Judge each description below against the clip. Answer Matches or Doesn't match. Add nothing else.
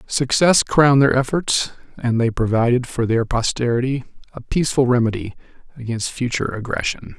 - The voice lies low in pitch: Matches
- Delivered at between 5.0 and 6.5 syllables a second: Matches